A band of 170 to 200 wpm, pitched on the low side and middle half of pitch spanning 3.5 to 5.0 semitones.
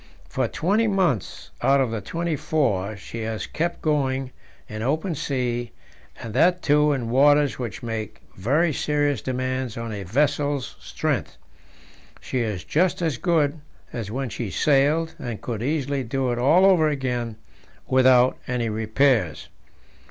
No: average, 145 wpm; low, 130 Hz; average, 4.3 semitones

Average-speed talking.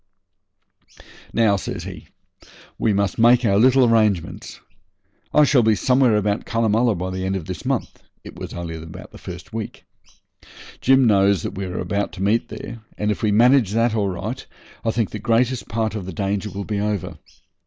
Yes: average, 180 wpm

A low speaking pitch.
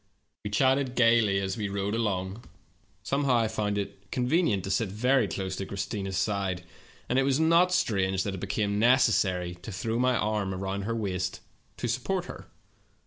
Yes: low, 105 Hz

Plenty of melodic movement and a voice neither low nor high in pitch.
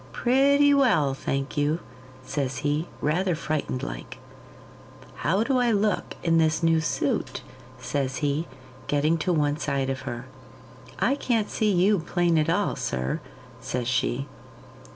Yes: wide, 5.9 semitones; medium, 155 Hz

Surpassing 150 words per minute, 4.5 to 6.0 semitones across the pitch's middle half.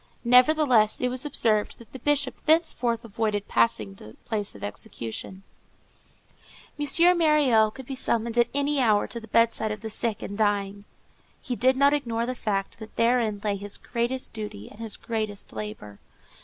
No: average, 170 wpm; average, 3.6 semitones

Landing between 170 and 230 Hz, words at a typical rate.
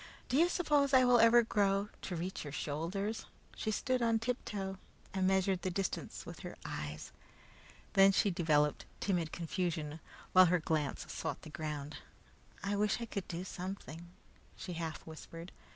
Yes: high, 190 Hz; average, 160 wpm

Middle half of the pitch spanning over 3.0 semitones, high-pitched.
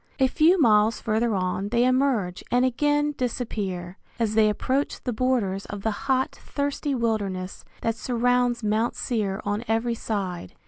Yes: average, 3.7 semitones; high, 230 Hz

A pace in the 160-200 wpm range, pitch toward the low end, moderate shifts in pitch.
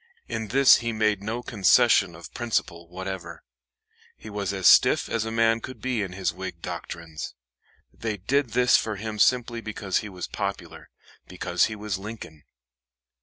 Yes: average, 165 wpm; low, 105 Hz; average, 3.2 semitones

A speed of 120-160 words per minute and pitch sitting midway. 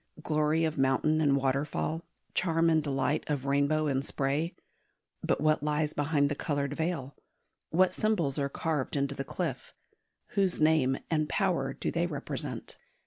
Yes: average, 150 wpm; medium, 150 Hz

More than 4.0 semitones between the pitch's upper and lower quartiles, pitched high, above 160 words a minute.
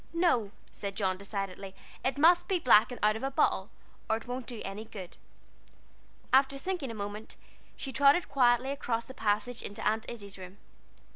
Yes: average, 4.8 semitones; high, 230 Hz; average, 180 wpm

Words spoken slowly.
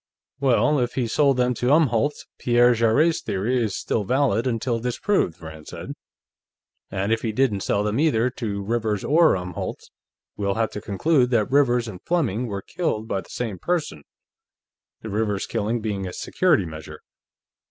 No: average, 165 wpm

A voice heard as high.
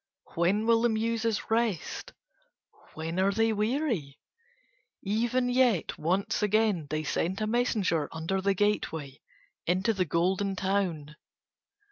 Yes: high, 200 Hz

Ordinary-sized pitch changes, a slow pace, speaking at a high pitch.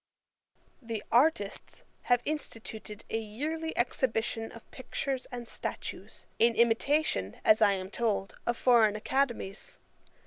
Yes: average, 3.2 semitones; slow, 115 wpm; high, 230 Hz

